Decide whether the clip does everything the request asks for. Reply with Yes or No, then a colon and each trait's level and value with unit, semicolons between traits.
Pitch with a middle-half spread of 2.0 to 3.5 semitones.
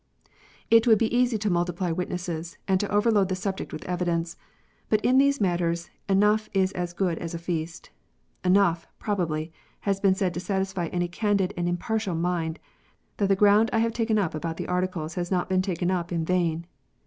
Yes: average, 3.0 semitones